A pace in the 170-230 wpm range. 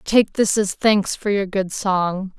Yes: average, 200 wpm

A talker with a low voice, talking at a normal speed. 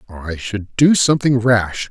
Yes: low, 115 Hz; average, 155 wpm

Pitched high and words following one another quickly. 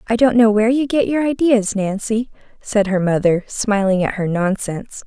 No: high, 215 Hz; average, 190 wpm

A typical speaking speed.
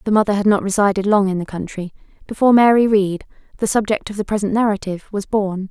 No: fast, 210 wpm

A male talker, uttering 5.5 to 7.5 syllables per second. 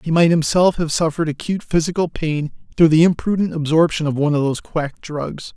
Yes: male; 6.0 syllables/s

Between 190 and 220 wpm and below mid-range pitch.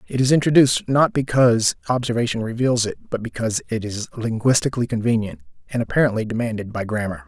No: average, 155 wpm; low, 120 Hz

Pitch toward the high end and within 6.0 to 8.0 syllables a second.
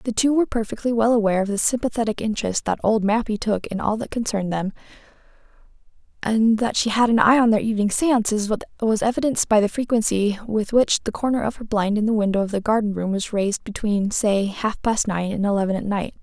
Yes: high, 215 Hz; 6.1 syllables/s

